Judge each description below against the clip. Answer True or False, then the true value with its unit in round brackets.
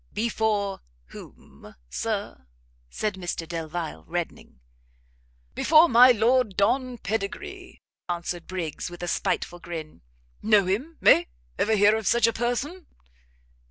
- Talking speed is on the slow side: True (120 wpm)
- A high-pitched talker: True (205 Hz)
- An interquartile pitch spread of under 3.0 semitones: False (5.4 semitones)